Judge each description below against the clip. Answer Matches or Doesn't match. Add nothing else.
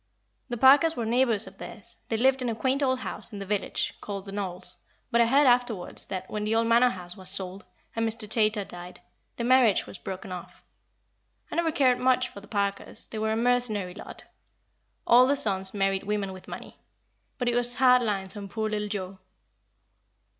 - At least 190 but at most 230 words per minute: Matches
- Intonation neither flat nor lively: Matches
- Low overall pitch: Doesn't match